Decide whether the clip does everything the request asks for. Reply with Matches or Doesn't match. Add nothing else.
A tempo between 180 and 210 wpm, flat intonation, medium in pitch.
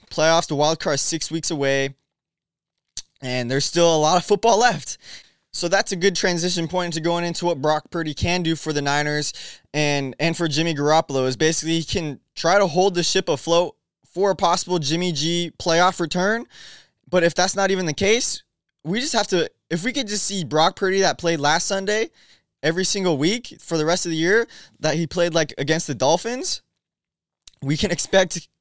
Doesn't match